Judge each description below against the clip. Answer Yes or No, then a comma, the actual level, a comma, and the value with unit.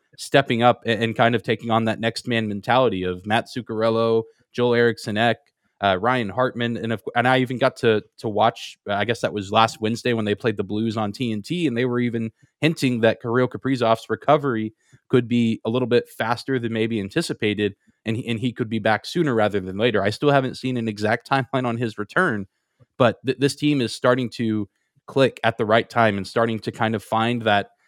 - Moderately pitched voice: No, low, 115 Hz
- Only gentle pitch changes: Yes, narrow, 2.3 semitones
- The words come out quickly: Yes, fast, 215 wpm